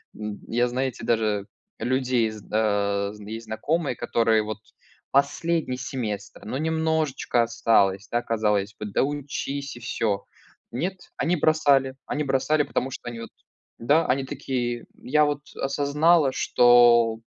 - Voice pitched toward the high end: No, low, 125 Hz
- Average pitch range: Yes, average, 4.2 semitones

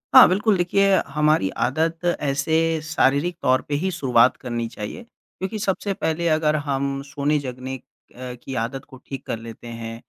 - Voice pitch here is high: No, medium, 140 Hz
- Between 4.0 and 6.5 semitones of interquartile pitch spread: Yes, average, 4.9 semitones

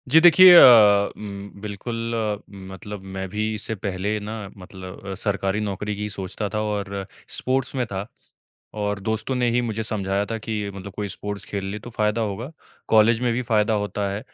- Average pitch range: No, narrow, 2.1 semitones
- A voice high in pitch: No, low, 105 Hz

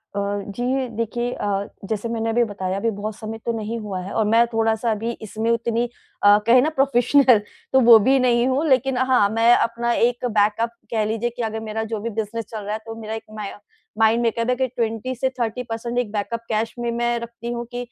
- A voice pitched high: Yes, high, 230 Hz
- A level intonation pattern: Yes, narrow, 1.7 semitones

